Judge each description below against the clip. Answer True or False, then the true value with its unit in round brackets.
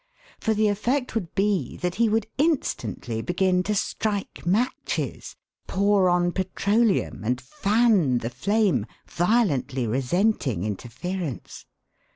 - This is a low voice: False (190 Hz)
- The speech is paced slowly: True (115 wpm)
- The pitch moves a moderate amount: False (7.8 semitones)